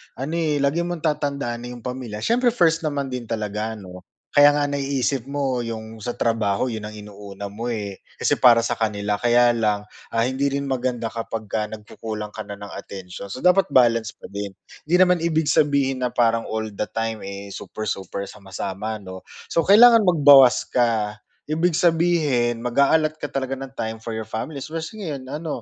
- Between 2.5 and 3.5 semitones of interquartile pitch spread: No, average, 5.1 semitones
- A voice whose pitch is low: Yes, low, 120 Hz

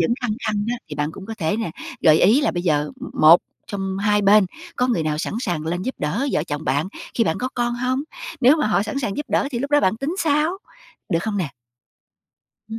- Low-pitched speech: No, high, 205 Hz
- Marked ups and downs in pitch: Yes, wide, 7.1 semitones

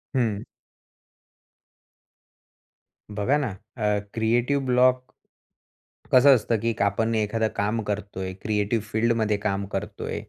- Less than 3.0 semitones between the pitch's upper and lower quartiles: Yes, narrow, 2.4 semitones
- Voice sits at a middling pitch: No, low, 110 Hz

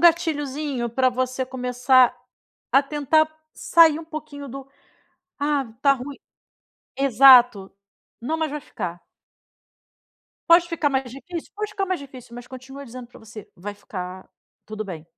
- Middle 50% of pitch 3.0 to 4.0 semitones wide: Yes, average, 3.7 semitones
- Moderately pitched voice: No, very high, 270 Hz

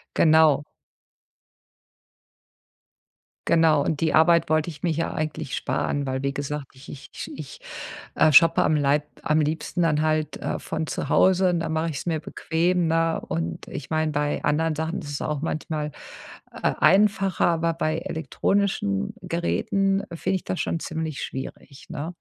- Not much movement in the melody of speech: Yes, narrow, 2.0 semitones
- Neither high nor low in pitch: Yes, medium, 160 Hz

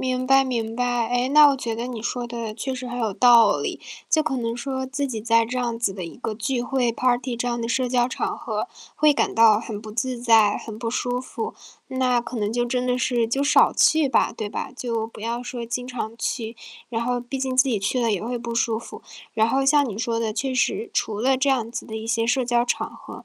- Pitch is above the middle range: Yes, high, 240 Hz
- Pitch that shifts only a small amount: Yes, narrow, 2.0 semitones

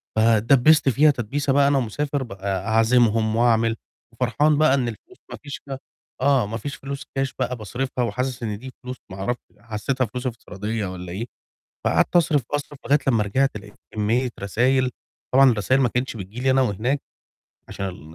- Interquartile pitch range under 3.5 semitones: No, average, 3.8 semitones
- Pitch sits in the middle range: No, low, 125 Hz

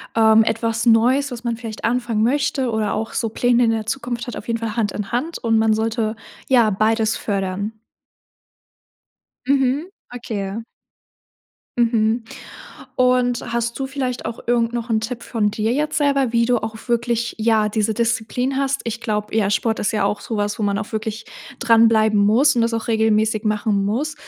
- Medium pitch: No, high, 230 Hz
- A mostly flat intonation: Yes, narrow, 2.0 semitones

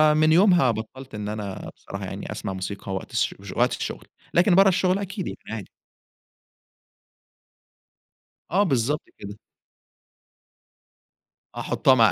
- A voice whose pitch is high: No, low, 130 Hz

